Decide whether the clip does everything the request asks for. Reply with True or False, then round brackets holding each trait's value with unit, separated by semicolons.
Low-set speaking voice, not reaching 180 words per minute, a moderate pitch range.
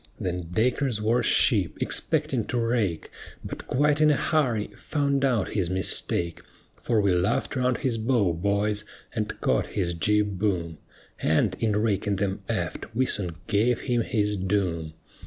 True (105 Hz; 155 wpm; 4.4 semitones)